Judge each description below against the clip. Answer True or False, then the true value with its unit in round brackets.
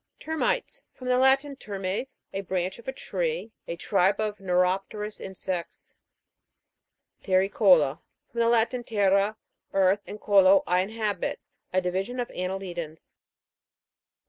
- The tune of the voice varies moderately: True (3.8 semitones)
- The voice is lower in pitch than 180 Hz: False (195 Hz)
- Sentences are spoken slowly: True (125 wpm)